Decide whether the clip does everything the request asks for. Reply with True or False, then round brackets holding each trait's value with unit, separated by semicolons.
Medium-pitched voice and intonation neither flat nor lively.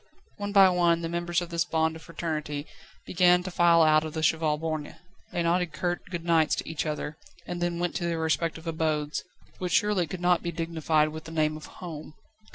False (165 Hz; 1.9 semitones)